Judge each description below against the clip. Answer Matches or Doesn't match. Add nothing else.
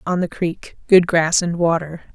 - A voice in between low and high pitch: Matches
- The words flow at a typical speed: Matches